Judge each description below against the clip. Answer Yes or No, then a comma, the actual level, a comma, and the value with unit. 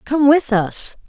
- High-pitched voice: Yes, very high, 260 Hz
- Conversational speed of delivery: Yes, average, 165 wpm